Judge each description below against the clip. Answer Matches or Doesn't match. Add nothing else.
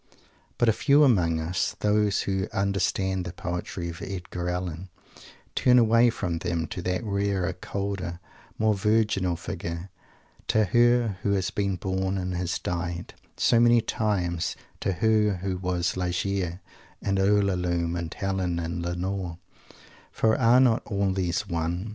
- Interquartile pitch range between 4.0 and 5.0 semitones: Doesn't match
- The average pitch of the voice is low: Matches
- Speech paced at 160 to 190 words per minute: Doesn't match